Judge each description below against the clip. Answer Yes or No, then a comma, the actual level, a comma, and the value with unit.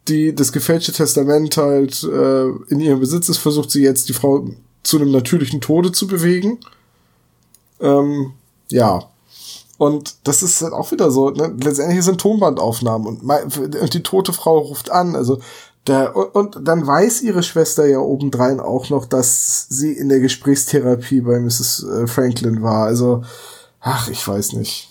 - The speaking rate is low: No, average, 155 wpm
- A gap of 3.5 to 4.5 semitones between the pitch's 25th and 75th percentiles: Yes, average, 3.8 semitones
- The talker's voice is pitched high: No, medium, 140 Hz